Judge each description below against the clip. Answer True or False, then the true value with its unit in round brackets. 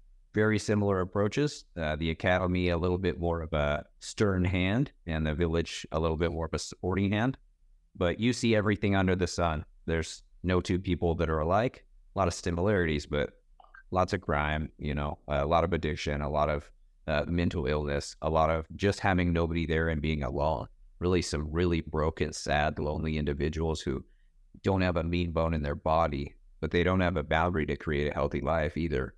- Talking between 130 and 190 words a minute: False (200 wpm)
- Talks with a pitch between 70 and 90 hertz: True (85 Hz)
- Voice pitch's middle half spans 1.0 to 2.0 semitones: False (2.9 semitones)